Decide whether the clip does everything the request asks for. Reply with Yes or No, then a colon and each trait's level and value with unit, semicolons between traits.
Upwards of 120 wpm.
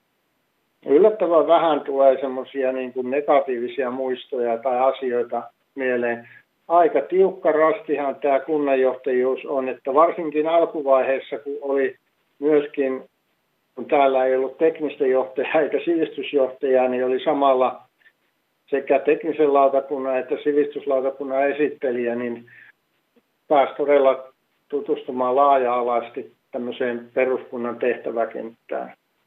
No: slow, 95 wpm